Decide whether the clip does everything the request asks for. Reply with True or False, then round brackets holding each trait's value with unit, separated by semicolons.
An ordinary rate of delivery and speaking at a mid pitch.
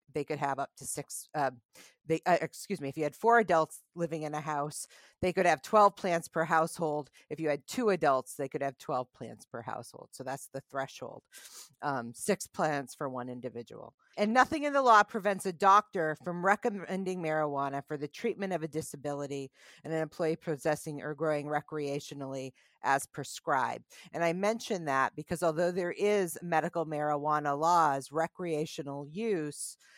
True (175 wpm; 155 Hz)